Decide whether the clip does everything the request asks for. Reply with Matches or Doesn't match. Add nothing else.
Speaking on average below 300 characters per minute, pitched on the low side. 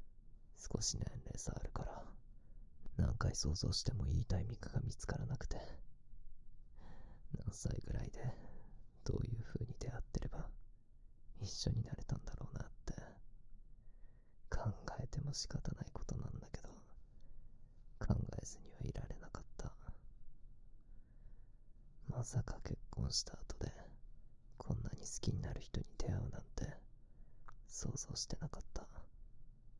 Matches